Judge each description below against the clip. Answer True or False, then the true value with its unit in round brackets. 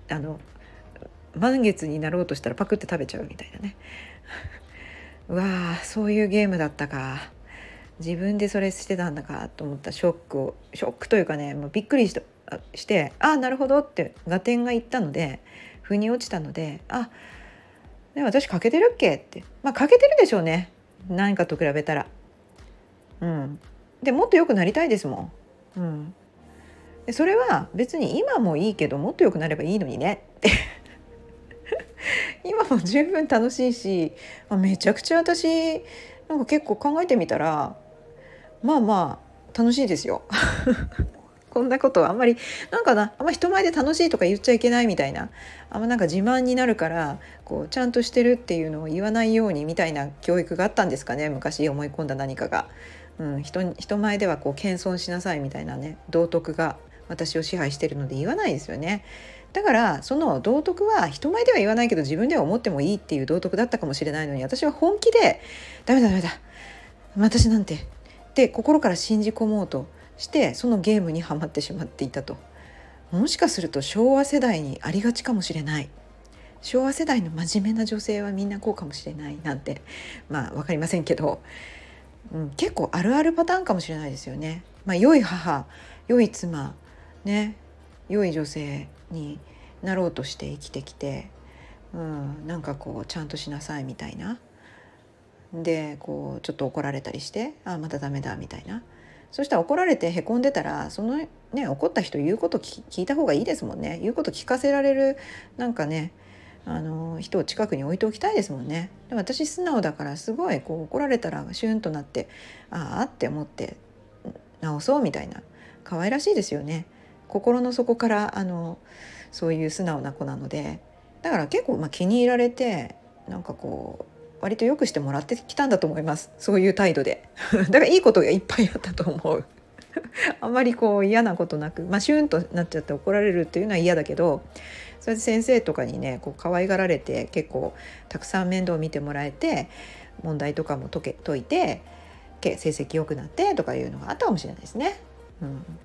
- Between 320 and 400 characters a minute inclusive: True (370 characters per minute)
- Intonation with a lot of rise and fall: True (7.9 semitones)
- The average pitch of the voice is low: False (180 Hz)